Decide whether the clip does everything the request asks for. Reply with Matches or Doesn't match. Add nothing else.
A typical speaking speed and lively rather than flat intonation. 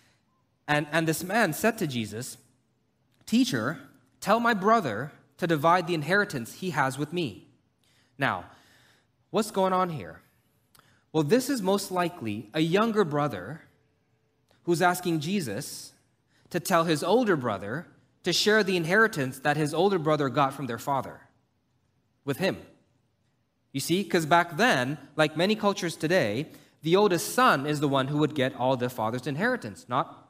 Matches